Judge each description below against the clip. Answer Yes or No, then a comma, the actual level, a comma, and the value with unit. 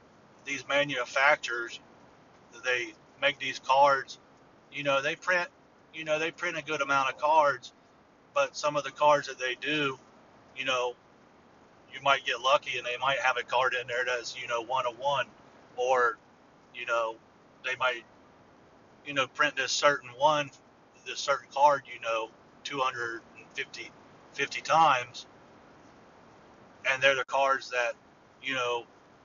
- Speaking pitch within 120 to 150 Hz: Yes, low, 135 Hz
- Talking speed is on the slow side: No, average, 150 wpm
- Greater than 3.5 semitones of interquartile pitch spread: No, average, 3.2 semitones